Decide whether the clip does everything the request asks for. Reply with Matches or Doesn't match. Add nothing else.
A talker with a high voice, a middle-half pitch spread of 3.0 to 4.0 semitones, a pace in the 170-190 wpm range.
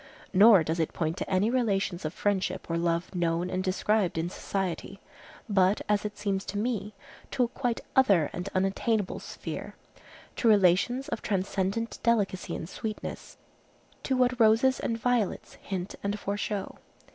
Doesn't match